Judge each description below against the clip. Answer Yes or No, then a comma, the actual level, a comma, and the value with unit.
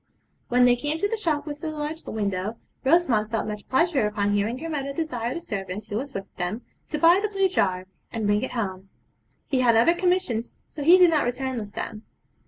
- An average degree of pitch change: No, wide, 7.1 semitones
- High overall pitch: Yes, very high, 250 Hz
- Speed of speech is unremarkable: No, fast, 215 wpm